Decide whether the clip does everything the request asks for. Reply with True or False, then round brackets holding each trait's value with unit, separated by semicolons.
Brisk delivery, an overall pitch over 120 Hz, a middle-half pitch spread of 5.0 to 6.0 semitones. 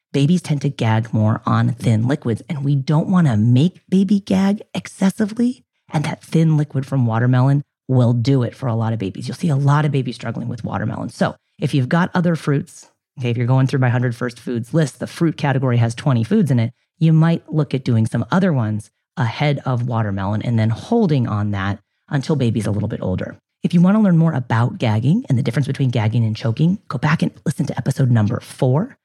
True (225 wpm; 135 Hz; 5.3 semitones)